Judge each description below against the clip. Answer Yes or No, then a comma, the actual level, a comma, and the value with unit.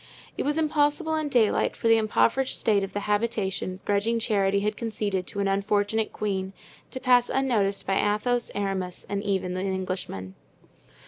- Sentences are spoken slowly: No, average, 165 wpm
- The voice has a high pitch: Yes, high, 205 Hz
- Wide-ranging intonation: No, average, 3.1 semitones